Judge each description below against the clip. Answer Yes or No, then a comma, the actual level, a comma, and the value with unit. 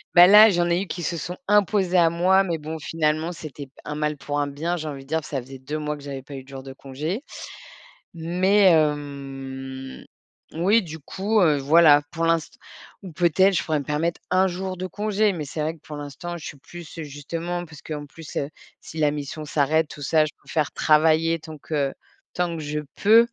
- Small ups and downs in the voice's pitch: No, average, 3.1 semitones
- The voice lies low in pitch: No, medium, 155 Hz